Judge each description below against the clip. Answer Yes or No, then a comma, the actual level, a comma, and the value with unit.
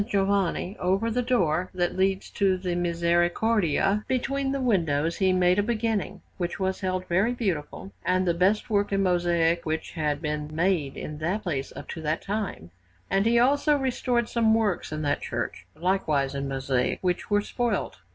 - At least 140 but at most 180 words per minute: Yes, average, 175 wpm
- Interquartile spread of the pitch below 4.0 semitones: No, average, 4.3 semitones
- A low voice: No, medium, 185 Hz